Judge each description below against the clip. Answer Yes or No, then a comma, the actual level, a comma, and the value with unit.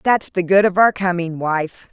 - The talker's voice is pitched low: No, medium, 180 Hz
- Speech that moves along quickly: Yes, fast, 220 wpm